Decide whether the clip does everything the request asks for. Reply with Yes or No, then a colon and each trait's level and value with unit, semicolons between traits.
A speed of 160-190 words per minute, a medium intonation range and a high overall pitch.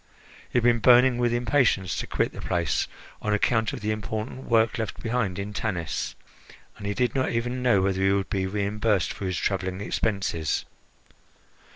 No: average, 180 wpm; average, 3.7 semitones; low, 105 Hz